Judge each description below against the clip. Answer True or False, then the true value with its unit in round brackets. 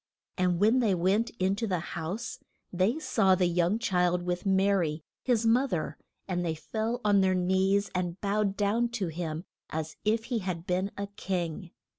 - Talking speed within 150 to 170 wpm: False (185 wpm)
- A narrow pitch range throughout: False (3.1 semitones)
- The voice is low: False (190 Hz)